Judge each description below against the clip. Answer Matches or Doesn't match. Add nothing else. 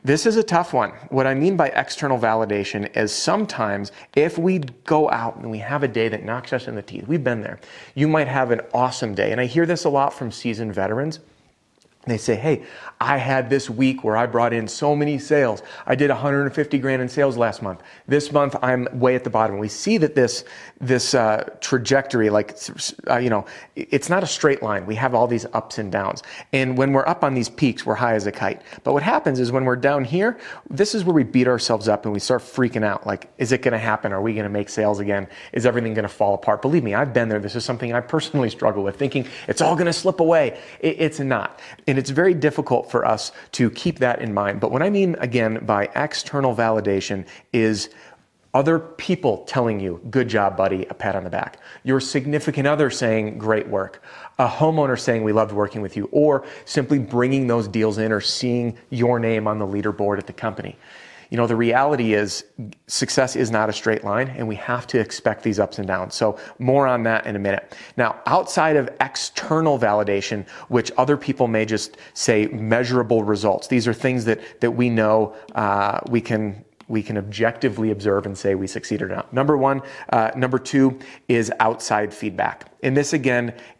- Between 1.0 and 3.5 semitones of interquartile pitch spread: Doesn't match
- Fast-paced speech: Matches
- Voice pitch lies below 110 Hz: Doesn't match